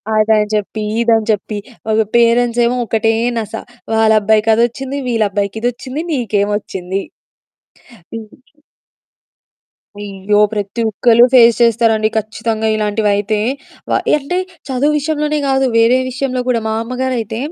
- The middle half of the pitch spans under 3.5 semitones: Yes, narrow, 2.6 semitones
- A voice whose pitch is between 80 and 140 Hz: No, high, 225 Hz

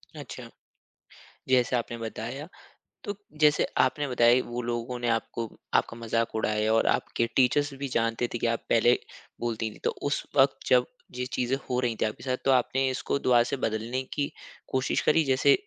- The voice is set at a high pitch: No, low, 125 Hz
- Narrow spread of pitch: Yes, narrow, 2.3 semitones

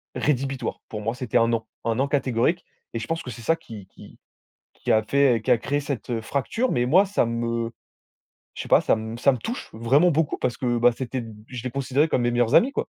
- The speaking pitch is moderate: No, low, 125 Hz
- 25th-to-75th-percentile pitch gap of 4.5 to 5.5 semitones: No, average, 3.4 semitones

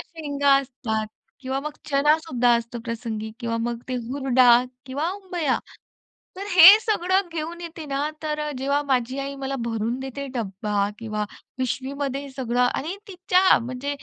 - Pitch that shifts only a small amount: No, average, 4.2 semitones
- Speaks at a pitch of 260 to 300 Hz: Yes, very high, 275 Hz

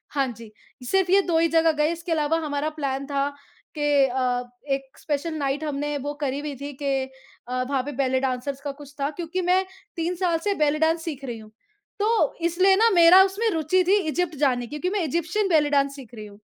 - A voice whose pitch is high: Yes, very high, 295 Hz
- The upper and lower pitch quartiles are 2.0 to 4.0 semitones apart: Yes, average, 3.7 semitones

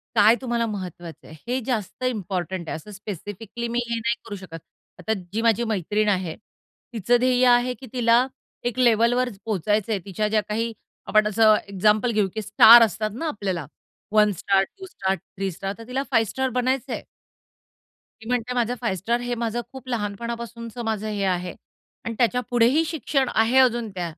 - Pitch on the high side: Yes, high, 225 Hz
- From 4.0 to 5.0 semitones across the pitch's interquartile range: No, average, 3.3 semitones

